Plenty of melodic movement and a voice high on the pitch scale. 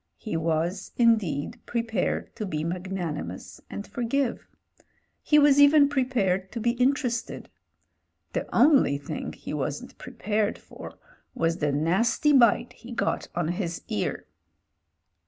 Yes: wide, 6.7 semitones; high, 210 Hz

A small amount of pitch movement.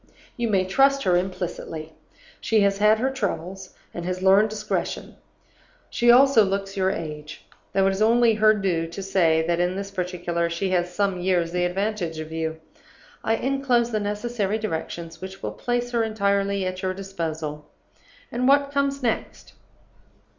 No: average, 3.8 semitones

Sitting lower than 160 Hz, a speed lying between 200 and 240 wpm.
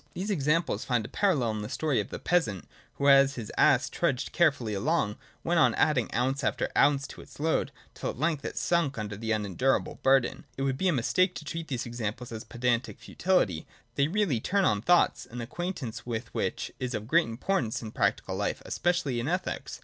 Yes: low, 135 Hz; fast, 205 wpm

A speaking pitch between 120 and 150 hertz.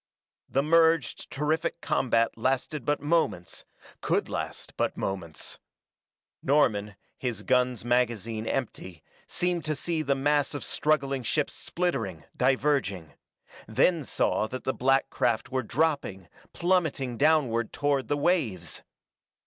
Yes: low, 135 Hz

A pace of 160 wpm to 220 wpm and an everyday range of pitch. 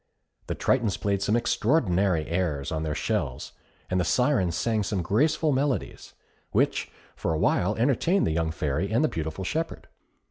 No: average, 165 wpm; wide, 7.2 semitones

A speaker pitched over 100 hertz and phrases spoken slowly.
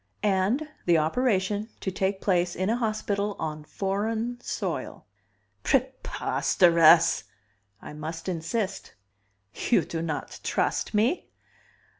Yes: high, 190 Hz; slow, 105 wpm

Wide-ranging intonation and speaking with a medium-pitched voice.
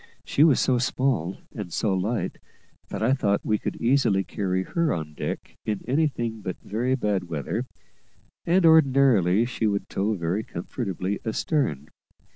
No: wide, 5.7 semitones; low, 110 Hz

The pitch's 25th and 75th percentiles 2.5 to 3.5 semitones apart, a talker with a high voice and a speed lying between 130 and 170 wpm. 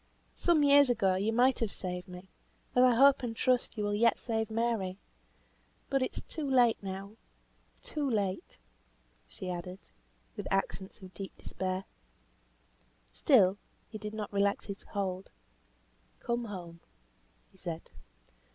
No: average, 4.2 semitones; high, 205 Hz; average, 140 wpm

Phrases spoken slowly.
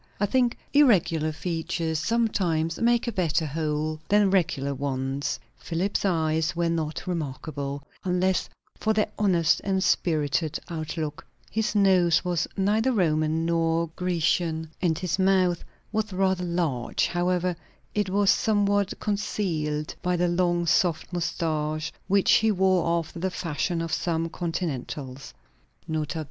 Yes: slow, 130 wpm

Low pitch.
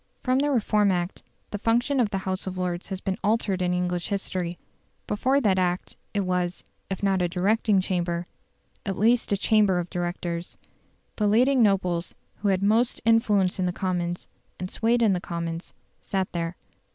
No: high, 190 Hz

